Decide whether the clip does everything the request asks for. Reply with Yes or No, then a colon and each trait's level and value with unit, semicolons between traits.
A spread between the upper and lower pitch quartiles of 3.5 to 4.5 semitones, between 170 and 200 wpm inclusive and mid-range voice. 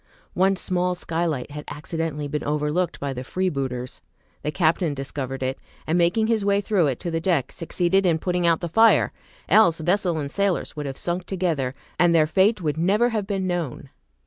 Yes: average, 3.9 semitones; average, 190 wpm; medium, 170 Hz